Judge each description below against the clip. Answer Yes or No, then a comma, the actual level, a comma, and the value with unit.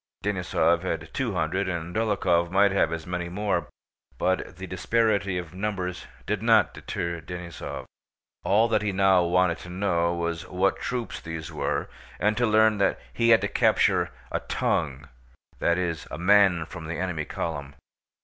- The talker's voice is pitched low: Yes, very low, 90 Hz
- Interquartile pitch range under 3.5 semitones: Yes, average, 3.0 semitones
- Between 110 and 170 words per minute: Yes, average, 160 wpm